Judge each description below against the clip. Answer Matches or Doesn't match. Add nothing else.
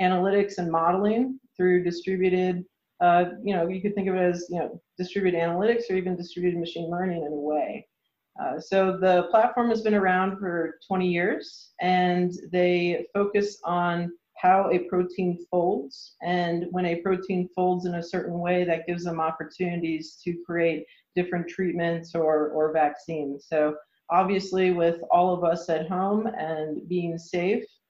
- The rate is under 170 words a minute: Matches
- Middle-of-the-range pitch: Matches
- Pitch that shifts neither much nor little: Doesn't match